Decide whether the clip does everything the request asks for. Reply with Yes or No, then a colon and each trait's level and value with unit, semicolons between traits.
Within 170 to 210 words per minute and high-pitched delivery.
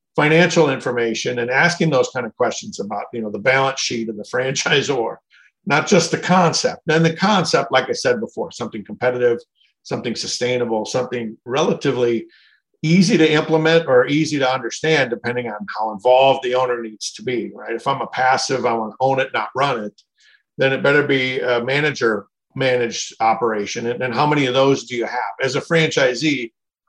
No: average, 185 wpm; low, 130 Hz